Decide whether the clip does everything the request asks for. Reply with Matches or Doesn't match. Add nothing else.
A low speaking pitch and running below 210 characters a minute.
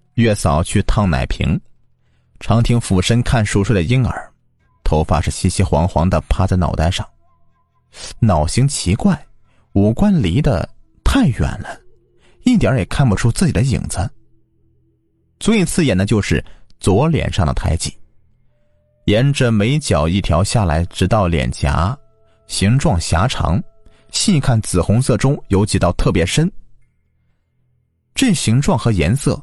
Matches